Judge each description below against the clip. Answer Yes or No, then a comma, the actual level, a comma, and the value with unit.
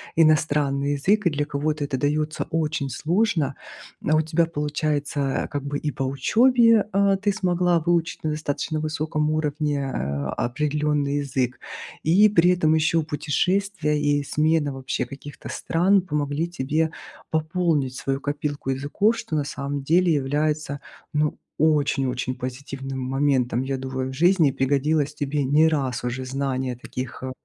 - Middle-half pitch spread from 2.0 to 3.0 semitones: Yes, average, 2.7 semitones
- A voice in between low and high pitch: Yes, medium, 150 Hz